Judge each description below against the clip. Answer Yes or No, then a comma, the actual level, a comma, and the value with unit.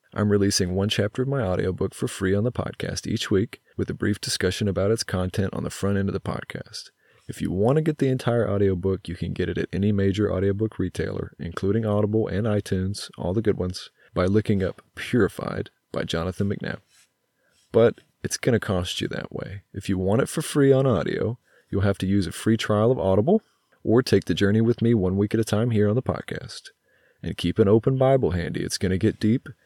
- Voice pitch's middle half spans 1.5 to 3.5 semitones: Yes, average, 2.9 semitones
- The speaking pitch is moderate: No, low, 100 Hz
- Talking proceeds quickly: Yes, fast, 225 wpm